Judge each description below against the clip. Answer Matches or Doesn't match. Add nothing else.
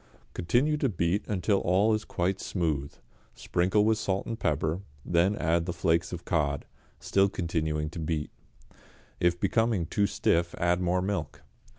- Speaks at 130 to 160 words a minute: Matches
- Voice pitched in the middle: Doesn't match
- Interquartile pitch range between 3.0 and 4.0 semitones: Matches